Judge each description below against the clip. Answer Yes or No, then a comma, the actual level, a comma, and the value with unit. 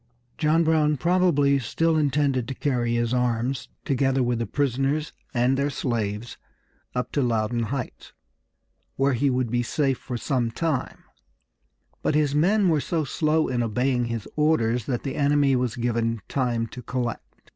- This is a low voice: Yes, low, 130 Hz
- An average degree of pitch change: Yes, average, 3.6 semitones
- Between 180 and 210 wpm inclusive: No, average, 155 wpm